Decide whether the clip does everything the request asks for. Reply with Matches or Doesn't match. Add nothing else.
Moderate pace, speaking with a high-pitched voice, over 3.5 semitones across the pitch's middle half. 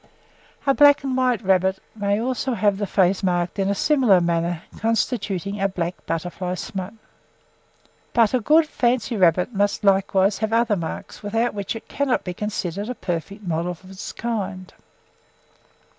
Matches